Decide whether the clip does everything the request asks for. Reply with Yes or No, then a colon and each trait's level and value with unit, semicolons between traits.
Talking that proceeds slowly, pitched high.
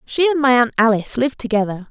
No: fast, 220 wpm; high, 245 Hz